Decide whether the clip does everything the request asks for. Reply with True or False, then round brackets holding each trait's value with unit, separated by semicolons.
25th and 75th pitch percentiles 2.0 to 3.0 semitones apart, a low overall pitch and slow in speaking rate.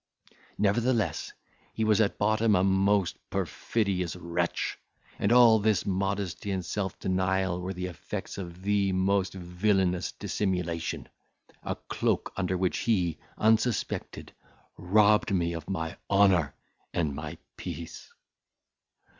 True (2.5 semitones; 95 Hz; 120 wpm)